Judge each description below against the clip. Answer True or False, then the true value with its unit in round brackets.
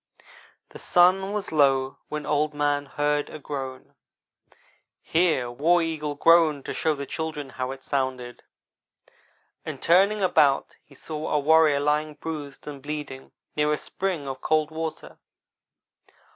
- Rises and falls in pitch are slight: True (2.3 semitones)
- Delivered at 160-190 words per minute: False (140 wpm)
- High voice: False (150 Hz)